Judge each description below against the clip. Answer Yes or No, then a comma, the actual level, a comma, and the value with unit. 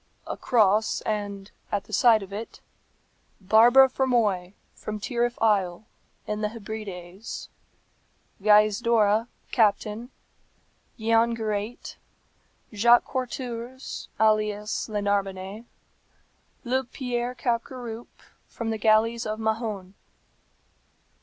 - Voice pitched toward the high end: Yes, high, 220 Hz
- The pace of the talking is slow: Yes, slow, 90 wpm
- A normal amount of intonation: No, narrow, 2.3 semitones